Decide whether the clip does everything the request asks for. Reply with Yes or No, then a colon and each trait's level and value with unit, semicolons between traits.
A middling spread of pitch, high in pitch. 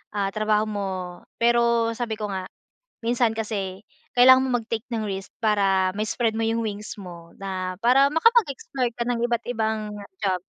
Yes: average, 3.0 semitones; high, 220 Hz